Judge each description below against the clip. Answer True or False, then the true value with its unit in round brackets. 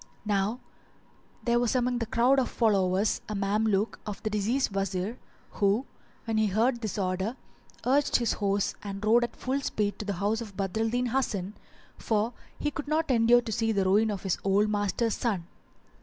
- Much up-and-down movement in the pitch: False (3.2 semitones)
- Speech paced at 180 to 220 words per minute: True (185 wpm)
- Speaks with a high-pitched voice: True (215 Hz)